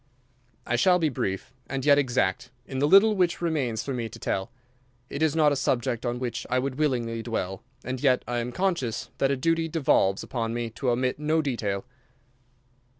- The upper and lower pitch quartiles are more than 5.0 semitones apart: No, average, 4.2 semitones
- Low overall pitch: Yes, low, 130 Hz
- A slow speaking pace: No, average, 195 wpm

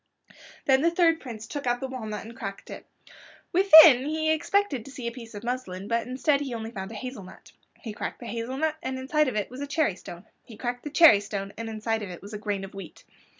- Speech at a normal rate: No, fast, 250 wpm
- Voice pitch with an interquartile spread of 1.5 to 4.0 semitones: No, average, 5.1 semitones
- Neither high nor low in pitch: No, high, 240 Hz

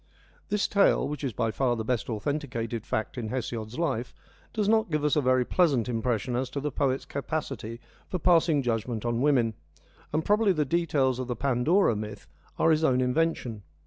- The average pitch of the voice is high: No, low, 130 Hz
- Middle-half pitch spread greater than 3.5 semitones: Yes, average, 4.6 semitones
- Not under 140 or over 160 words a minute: No, average, 185 wpm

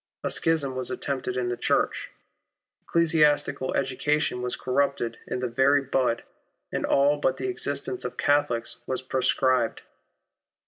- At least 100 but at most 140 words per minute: Yes, slow, 135 wpm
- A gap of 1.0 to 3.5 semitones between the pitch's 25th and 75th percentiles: Yes, narrow, 2.5 semitones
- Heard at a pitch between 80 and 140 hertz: Yes, low, 135 Hz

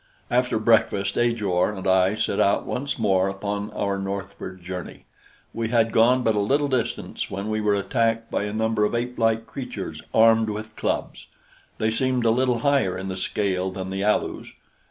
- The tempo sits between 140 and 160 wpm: No, average, 175 wpm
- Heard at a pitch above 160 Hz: No, low, 110 Hz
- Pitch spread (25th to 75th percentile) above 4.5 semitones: No, average, 2.9 semitones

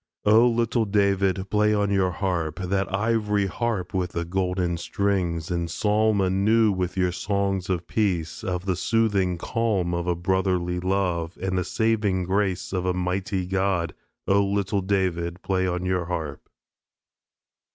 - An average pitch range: No, narrow, 2.1 semitones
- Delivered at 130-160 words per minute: Yes, average, 150 wpm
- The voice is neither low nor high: No, very low, 95 Hz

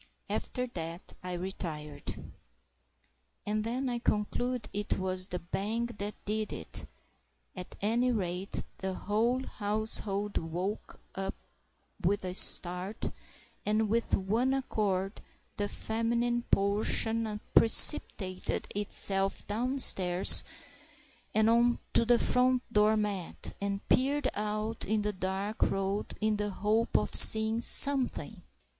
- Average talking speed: No, slow, 115 wpm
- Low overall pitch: No, high, 210 Hz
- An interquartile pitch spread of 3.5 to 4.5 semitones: No, average, 3.1 semitones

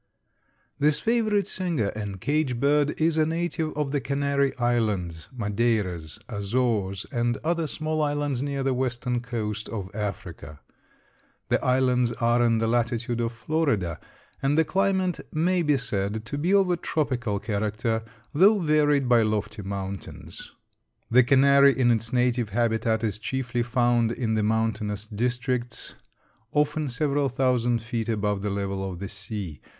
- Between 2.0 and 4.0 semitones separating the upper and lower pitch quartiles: No, average, 4.9 semitones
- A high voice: No, low, 120 Hz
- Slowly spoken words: No, average, 145 wpm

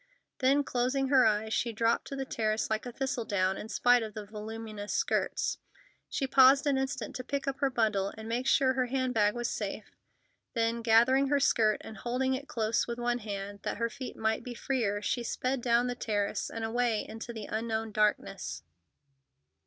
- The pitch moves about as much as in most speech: Yes, average, 3.0 semitones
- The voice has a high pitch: Yes, high, 235 Hz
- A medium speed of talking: Yes, average, 190 wpm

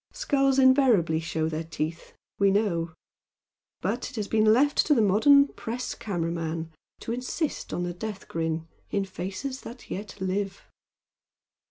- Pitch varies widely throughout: Yes, wide, 6.9 semitones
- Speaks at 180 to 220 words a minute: No, average, 150 wpm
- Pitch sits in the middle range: No, high, 200 Hz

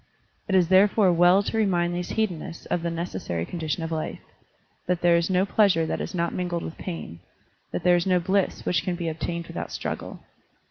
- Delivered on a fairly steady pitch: Yes, narrow, 2.0 semitones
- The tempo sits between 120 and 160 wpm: No, average, 200 wpm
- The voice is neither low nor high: Yes, medium, 175 Hz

